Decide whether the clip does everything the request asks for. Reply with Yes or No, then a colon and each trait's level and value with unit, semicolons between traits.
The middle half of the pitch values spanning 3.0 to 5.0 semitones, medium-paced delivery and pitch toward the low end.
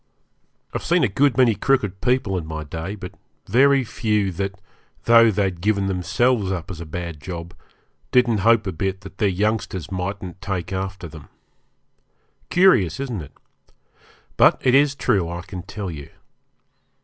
Yes: average, 4.4 semitones; average, 160 wpm; very low, 95 Hz